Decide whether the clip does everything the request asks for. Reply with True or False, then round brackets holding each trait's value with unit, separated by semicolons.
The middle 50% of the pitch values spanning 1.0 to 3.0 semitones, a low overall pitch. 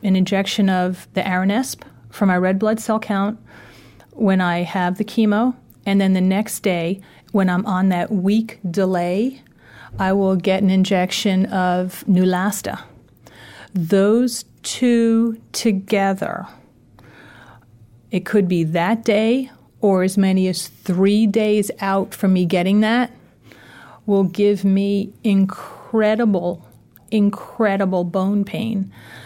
False (2.5 semitones; 195 Hz)